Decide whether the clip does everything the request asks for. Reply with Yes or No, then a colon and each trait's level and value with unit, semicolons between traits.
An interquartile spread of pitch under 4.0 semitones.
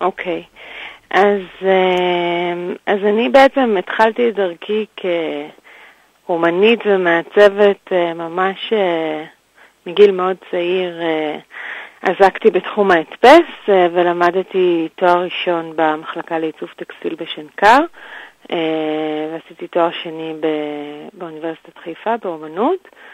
Yes: average, 3.6 semitones